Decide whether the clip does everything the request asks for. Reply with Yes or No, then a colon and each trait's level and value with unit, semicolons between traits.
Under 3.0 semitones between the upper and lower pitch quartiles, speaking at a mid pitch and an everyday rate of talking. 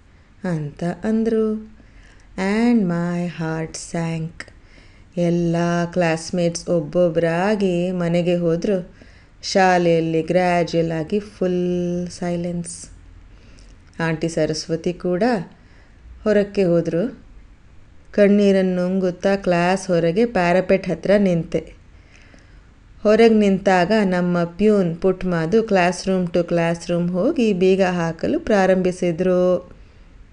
Yes: narrow, 2.6 semitones; medium, 175 Hz; average, 85 wpm